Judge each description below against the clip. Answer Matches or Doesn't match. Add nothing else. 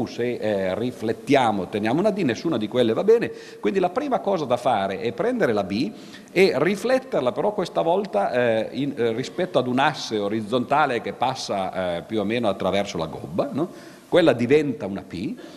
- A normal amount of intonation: Doesn't match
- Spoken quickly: Matches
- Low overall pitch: Matches